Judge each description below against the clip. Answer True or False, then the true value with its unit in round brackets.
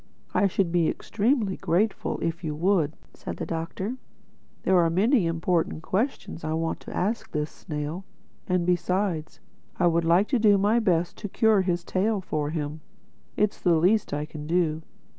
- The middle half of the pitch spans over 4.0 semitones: False (3.6 semitones)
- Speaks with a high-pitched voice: False (175 Hz)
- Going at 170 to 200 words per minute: True (175 wpm)